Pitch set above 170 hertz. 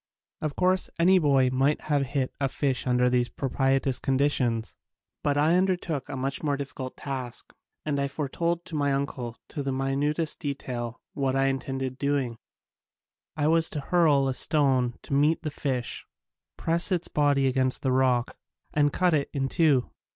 No: medium, 140 Hz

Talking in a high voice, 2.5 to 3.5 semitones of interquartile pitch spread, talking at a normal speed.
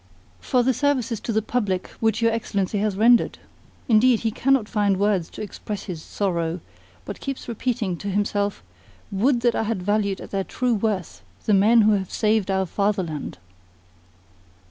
Yes: high, 210 Hz; average, 2.9 semitones; average, 165 wpm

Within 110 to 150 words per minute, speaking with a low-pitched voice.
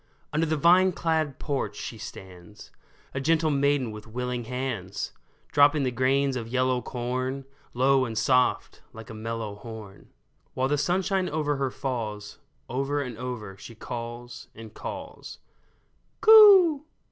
Yes: average, 145 wpm; low, 130 Hz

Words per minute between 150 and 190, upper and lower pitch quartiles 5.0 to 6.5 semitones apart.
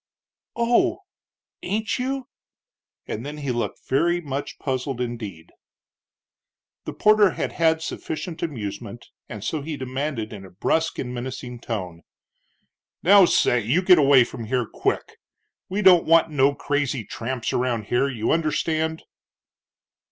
No: slow, 135 wpm; wide, 5.4 semitones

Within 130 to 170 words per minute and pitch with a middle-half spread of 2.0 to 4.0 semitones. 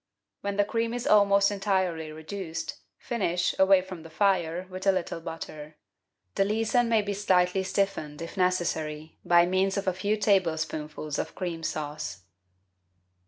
Yes: average, 150 wpm; average, 3.6 semitones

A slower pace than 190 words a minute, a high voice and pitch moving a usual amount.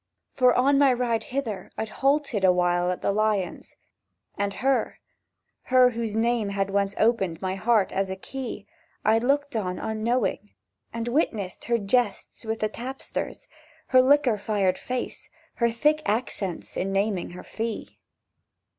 Yes: average, 145 wpm; high, 220 Hz; average, 4.1 semitones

